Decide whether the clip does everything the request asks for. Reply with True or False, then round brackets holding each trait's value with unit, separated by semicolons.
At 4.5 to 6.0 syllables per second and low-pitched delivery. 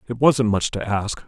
True (4.7 syllables/s; 110 Hz)